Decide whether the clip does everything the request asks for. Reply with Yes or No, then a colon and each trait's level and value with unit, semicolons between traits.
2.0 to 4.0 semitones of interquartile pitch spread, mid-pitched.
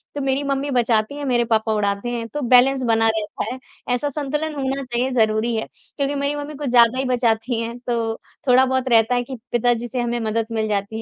No: average, 2.9 semitones; high, 240 Hz